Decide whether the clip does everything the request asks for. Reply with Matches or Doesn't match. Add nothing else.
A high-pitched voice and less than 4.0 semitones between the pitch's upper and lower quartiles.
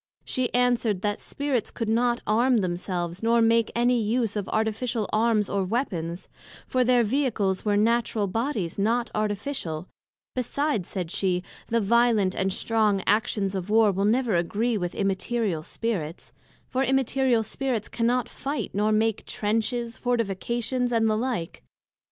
Matches